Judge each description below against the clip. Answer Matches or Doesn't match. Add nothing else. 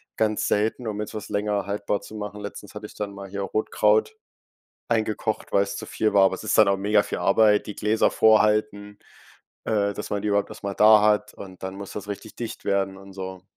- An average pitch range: Doesn't match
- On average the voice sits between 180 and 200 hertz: Doesn't match